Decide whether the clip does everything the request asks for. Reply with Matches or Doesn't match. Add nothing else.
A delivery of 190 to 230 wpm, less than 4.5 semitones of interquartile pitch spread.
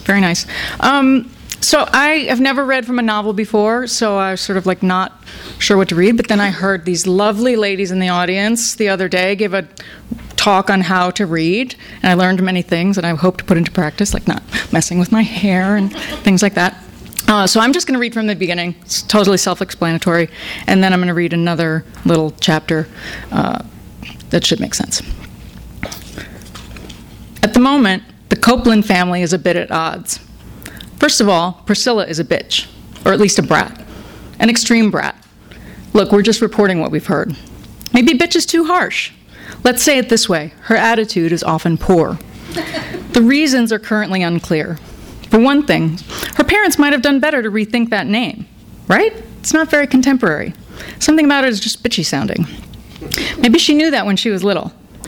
Doesn't match